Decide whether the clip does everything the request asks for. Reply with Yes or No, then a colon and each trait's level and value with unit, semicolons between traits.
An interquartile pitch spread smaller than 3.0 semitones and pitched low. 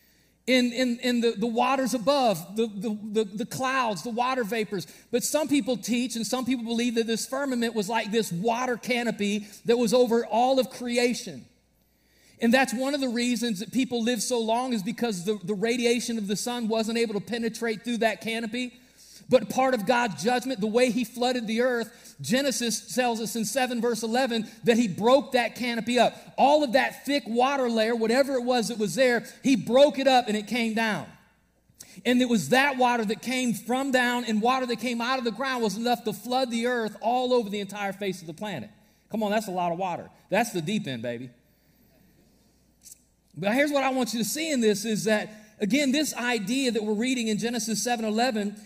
No: narrow, 2.5 semitones; high, 235 Hz